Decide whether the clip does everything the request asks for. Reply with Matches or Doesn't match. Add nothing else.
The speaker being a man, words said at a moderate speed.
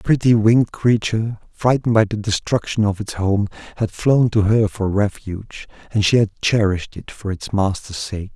Matches